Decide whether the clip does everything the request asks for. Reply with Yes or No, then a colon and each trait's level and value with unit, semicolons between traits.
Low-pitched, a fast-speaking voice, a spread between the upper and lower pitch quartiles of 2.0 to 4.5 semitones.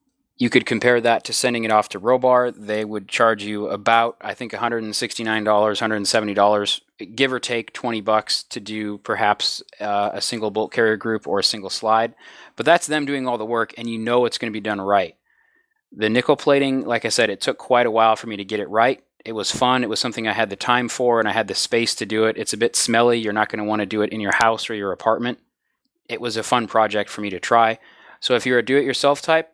Yes: low, 115 Hz; fast, 250 wpm; narrow, 2.5 semitones